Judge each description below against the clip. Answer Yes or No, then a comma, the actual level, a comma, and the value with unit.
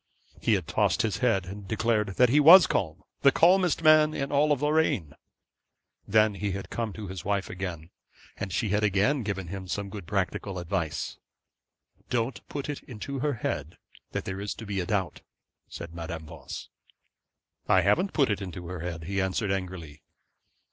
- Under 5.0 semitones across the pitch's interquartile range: No, average, 5.3 semitones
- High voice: No, low, 100 Hz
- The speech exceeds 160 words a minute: Yes, average, 175 wpm